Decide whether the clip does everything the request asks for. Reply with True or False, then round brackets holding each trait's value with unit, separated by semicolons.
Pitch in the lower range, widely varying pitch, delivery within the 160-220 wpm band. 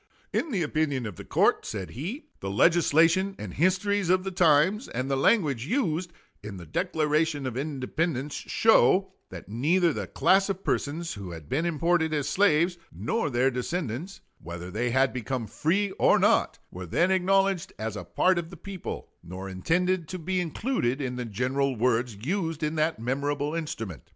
False (155 Hz; 6.4 semitones; 175 wpm)